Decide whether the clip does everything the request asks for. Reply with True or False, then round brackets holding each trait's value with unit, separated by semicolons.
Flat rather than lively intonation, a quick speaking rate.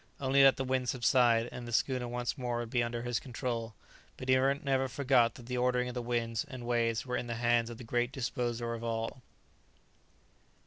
True (1.5 semitones; 210 wpm)